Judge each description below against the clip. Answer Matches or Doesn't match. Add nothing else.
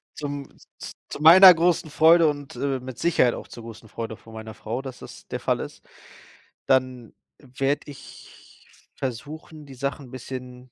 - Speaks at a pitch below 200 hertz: Matches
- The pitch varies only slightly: Doesn't match